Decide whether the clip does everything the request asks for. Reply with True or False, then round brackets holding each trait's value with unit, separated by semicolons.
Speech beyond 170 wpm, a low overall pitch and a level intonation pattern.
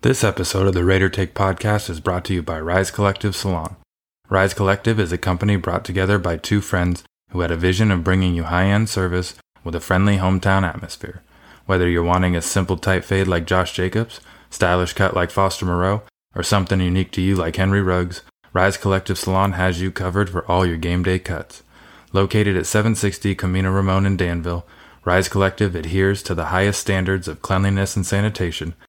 True (190 wpm; 95 Hz; 1.6 semitones)